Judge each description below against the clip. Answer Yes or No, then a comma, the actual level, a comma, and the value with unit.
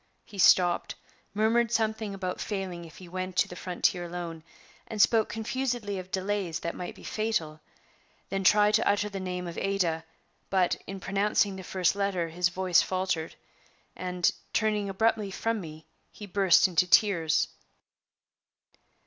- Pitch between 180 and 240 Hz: Yes, high, 190 Hz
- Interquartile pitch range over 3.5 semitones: No, average, 2.7 semitones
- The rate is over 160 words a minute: No, average, 150 wpm